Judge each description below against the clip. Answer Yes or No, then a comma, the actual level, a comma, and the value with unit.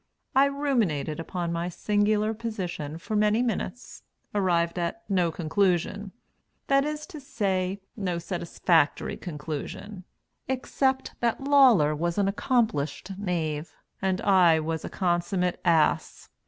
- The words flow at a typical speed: No, slow, 120 wpm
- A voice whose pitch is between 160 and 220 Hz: Yes, medium, 185 Hz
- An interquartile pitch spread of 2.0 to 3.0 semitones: No, average, 4.4 semitones